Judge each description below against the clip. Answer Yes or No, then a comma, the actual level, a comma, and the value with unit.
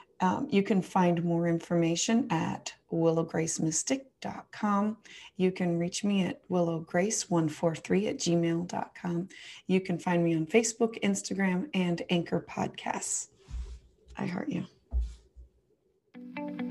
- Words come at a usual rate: No, slow, 105 wpm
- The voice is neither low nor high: Yes, medium, 175 Hz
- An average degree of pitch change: Yes, average, 3.6 semitones